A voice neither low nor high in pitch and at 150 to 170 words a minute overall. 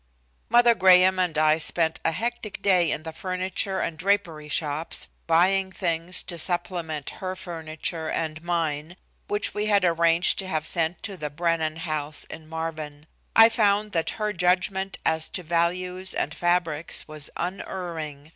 Yes: medium, 170 Hz; average, 155 wpm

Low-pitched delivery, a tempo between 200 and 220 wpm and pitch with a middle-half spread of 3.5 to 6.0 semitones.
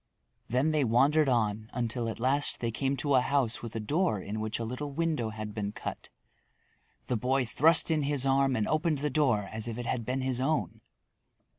Yes: low, 125 Hz; fast, 205 wpm; average, 4.3 semitones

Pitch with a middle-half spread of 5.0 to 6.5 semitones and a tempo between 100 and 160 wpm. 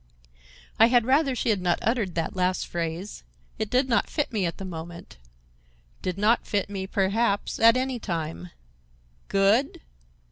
Yes: average, 5.3 semitones; average, 150 wpm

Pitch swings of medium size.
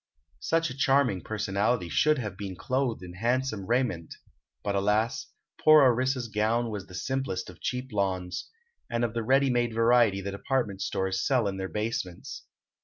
Yes: average, 4.7 semitones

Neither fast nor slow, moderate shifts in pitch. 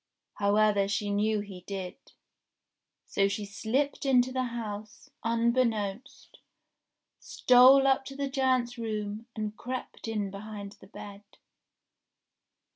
No: slow, 120 wpm; average, 3.7 semitones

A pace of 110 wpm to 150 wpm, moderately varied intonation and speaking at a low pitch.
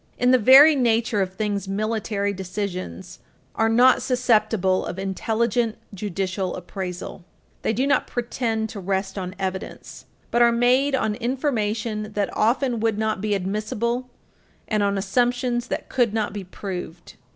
No: average, 145 wpm; average, 3.7 semitones; high, 215 Hz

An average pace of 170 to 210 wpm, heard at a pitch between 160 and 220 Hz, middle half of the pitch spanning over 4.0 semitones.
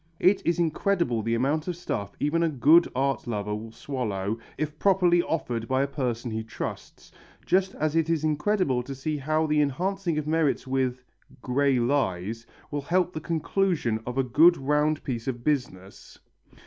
No: average, 175 wpm; medium, 140 Hz; average, 5.1 semitones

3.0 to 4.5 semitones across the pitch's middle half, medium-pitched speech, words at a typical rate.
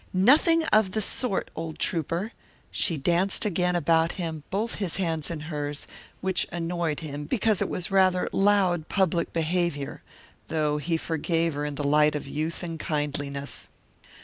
Yes: average, 3.8 semitones; medium, 165 Hz; average, 155 wpm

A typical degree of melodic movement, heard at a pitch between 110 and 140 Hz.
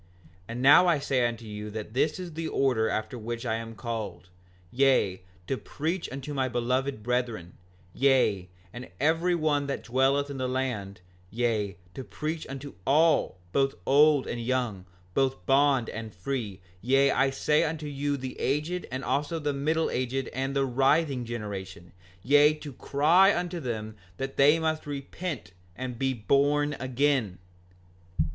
Yes: average, 4.0 semitones; low, 135 Hz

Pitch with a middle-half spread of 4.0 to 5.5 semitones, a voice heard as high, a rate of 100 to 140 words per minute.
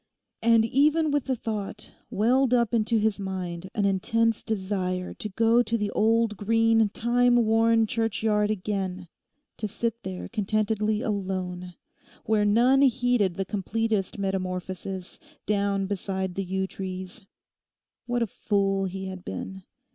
No: average, 3.1 semitones; high, 210 Hz; slow, 135 wpm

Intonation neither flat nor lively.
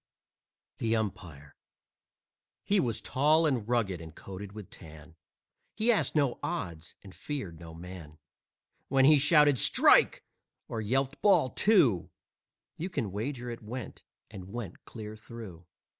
No: wide, 6.7 semitones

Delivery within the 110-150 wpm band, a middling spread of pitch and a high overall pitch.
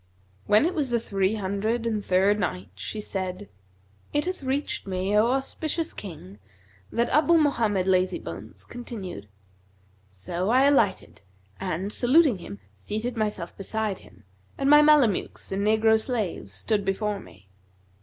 Yes: average, 140 wpm; average, 4.7 semitones; high, 210 Hz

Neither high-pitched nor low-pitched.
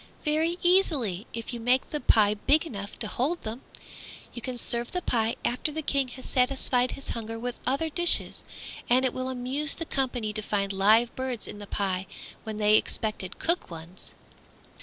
No: high, 245 Hz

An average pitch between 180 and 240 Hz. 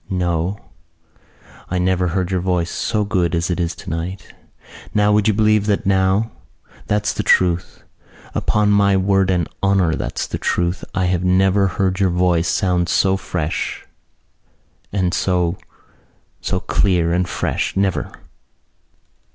No: very low, 95 Hz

